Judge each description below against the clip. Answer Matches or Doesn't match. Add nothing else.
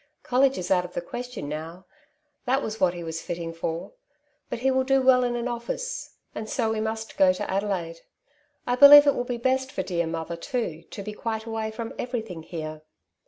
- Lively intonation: Matches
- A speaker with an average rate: Doesn't match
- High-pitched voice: Matches